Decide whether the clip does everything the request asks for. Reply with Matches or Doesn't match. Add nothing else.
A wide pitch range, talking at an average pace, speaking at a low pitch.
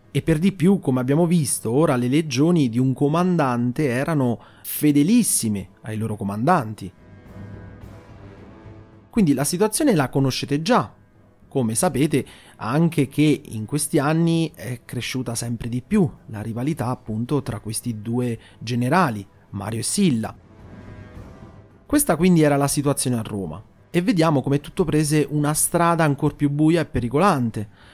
Matches